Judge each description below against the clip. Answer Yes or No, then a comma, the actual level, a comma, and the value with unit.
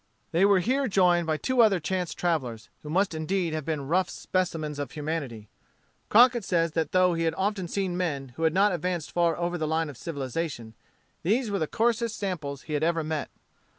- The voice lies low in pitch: No, medium, 170 Hz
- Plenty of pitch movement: No, average, 3.6 semitones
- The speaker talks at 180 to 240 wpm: Yes, average, 200 wpm